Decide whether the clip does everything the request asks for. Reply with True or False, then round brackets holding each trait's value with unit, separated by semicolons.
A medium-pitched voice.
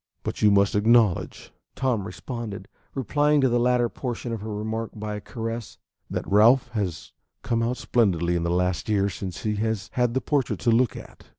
False (110 Hz)